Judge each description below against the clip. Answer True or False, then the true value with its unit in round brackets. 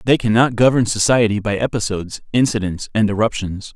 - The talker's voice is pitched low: True (110 Hz)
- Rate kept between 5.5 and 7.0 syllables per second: True (5.7 syllables/s)